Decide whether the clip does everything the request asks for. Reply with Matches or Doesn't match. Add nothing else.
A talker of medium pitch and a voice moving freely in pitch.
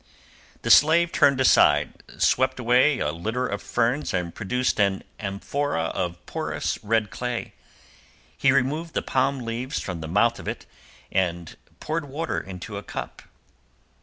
Doesn't match